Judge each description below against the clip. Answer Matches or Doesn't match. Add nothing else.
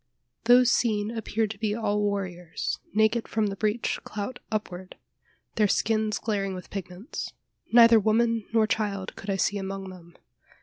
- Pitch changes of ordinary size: Doesn't match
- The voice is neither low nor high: Doesn't match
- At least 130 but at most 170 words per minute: Matches